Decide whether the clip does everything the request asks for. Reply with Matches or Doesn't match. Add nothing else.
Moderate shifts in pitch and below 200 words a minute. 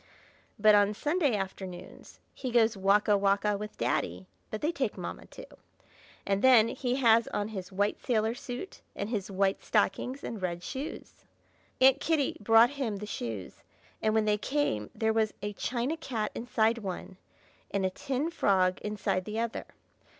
Matches